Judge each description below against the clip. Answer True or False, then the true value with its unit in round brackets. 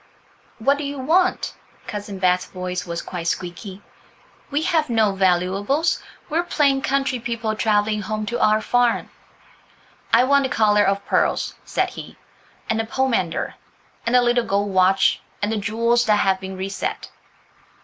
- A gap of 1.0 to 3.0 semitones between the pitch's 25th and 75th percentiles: False (4.6 semitones)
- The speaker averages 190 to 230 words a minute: False (160 wpm)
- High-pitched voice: True (215 Hz)